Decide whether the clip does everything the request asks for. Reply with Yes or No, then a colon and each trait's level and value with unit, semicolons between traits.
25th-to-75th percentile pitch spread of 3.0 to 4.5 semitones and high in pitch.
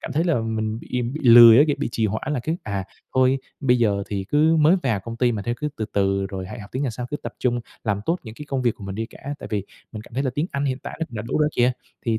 No: average, 4.2 semitones; low, 120 Hz